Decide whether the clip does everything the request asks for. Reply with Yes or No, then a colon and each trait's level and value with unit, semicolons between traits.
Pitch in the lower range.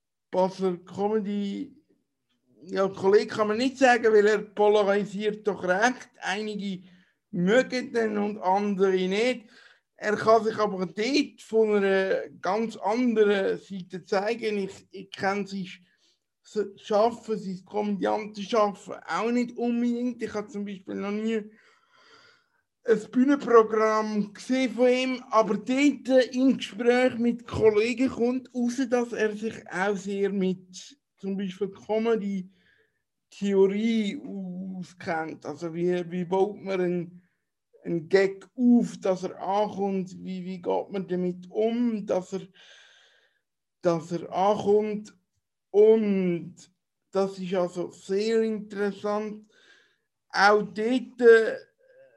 No: high, 210 Hz